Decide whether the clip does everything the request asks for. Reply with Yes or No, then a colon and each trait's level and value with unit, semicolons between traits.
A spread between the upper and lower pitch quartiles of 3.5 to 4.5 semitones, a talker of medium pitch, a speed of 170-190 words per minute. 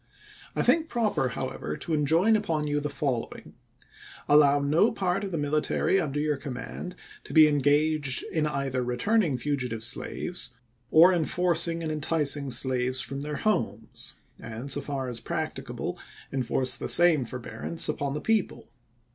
No: average, 4.1 semitones; medium, 145 Hz; average, 155 wpm